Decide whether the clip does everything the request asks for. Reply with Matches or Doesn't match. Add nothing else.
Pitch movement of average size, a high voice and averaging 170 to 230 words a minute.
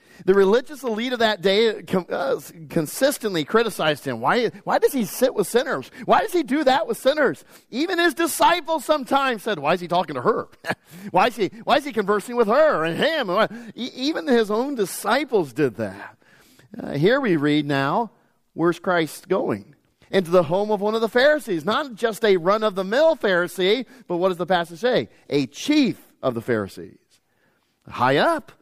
Doesn't match